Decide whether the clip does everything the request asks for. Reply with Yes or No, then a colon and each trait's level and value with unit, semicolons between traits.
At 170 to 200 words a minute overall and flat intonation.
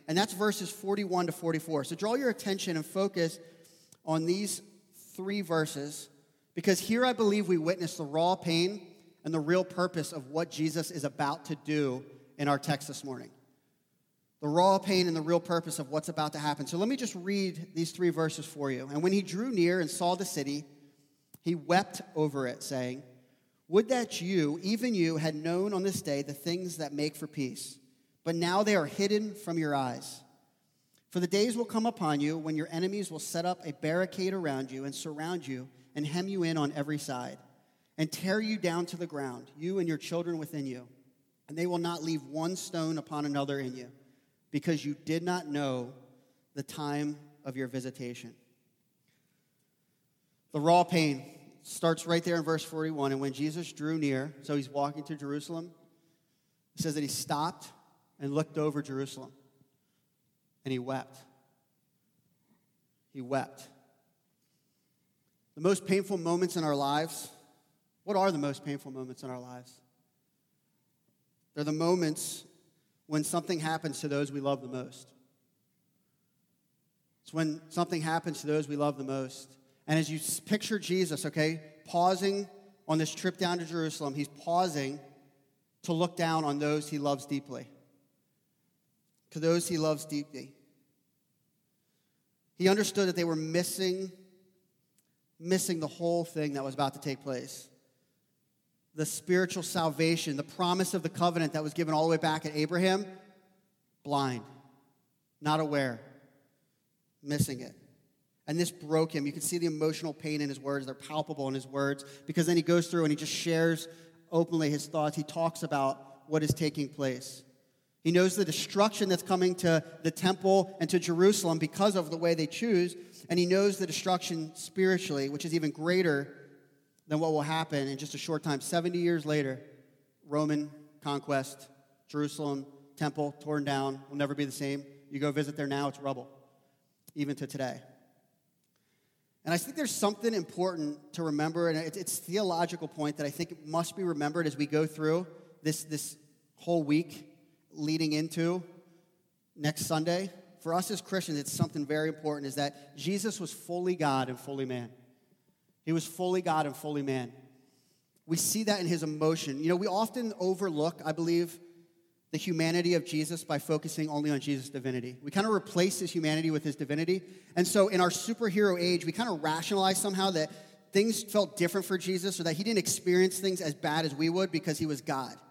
No: average, 175 wpm; average, 3.6 semitones